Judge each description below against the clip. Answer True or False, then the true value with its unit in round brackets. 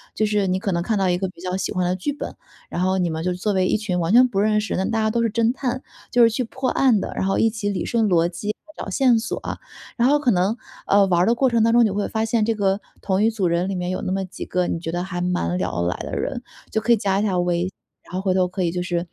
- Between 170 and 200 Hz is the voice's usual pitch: True (195 Hz)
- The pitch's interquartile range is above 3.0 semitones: True (3.8 semitones)